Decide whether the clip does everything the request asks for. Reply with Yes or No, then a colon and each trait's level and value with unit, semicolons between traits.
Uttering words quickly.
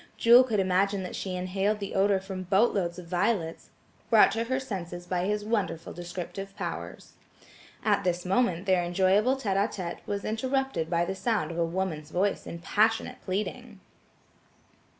No: average, 165 wpm